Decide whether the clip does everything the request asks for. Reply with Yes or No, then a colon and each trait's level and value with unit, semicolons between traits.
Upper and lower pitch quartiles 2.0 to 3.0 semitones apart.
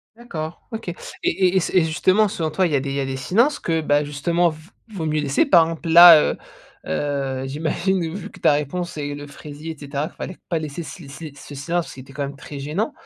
No: average, 3.4 semitones